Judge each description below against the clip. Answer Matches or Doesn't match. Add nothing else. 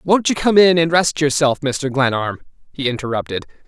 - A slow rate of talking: Doesn't match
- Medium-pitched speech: Matches